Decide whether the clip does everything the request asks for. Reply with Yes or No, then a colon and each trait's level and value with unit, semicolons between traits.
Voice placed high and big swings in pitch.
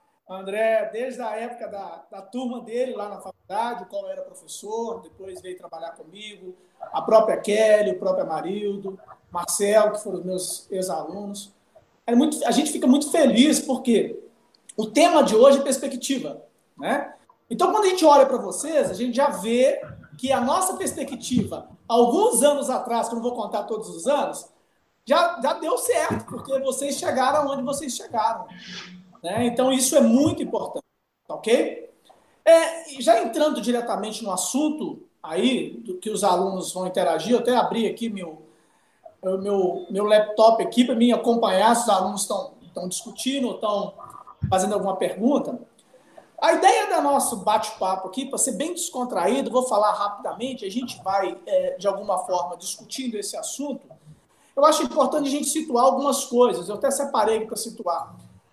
Yes: high, 235 Hz; wide, 5.8 semitones